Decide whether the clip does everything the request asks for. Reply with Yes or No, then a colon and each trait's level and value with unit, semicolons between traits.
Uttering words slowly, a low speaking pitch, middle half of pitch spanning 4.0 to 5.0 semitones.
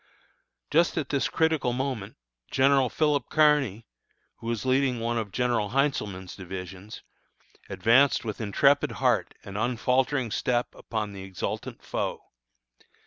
Yes: slow, 125 wpm; low, 120 Hz; average, 4.7 semitones